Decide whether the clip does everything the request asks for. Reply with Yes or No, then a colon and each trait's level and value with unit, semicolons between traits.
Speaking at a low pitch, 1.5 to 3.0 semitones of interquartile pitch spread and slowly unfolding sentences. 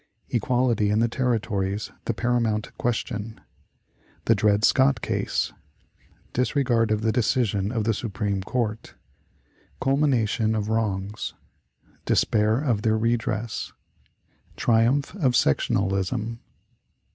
Yes: low, 115 Hz; narrow, 2.6 semitones; slow, 100 wpm